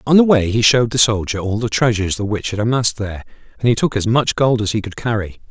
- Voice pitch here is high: No, low, 110 Hz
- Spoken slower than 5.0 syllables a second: No, 6.7 syllables/s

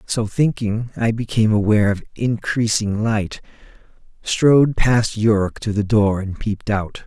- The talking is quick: No, average, 145 wpm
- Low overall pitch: Yes, low, 110 Hz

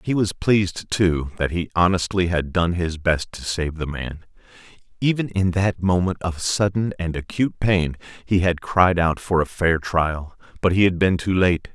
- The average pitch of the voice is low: Yes, very low, 90 Hz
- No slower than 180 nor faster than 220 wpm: Yes, average, 195 wpm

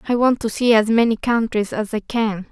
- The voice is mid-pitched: No, high, 225 Hz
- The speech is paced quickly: Yes, fast, 240 wpm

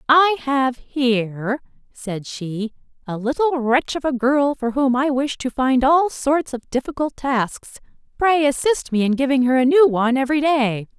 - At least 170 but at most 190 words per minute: Yes, average, 180 wpm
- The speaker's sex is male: No, female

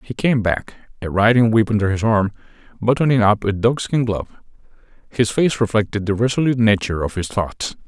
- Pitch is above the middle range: No, low, 110 Hz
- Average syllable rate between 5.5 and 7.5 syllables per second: Yes, 5.8 syllables/s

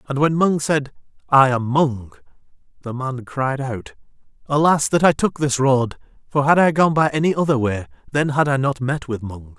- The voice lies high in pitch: No, low, 135 Hz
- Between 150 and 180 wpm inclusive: No, average, 200 wpm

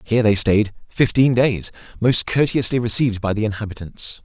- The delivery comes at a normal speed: Yes, average, 155 wpm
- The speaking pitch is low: Yes, low, 110 Hz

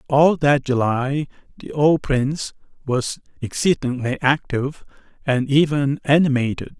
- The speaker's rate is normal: No, slow, 105 wpm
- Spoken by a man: Yes, male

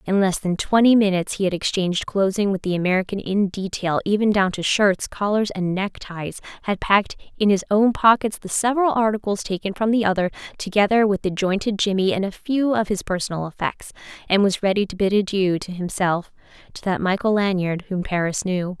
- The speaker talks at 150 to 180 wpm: No, average, 195 wpm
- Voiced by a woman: Yes, female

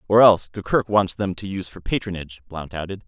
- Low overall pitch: Yes, very low, 95 Hz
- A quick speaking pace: Yes, fast, 215 wpm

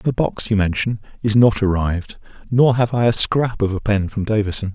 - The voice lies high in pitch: No, low, 110 Hz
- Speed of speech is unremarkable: No, fast, 215 wpm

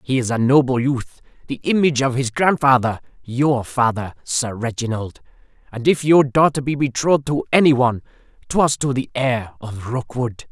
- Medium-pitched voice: No, low, 130 Hz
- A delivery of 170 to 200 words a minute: No, average, 160 wpm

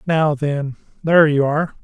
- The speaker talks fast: No, slow, 130 wpm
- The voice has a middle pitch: Yes, medium, 150 Hz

